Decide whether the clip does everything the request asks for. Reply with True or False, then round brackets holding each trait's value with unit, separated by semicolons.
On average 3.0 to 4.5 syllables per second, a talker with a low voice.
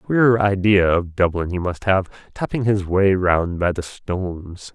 True (4.0 syllables/s; 95 Hz)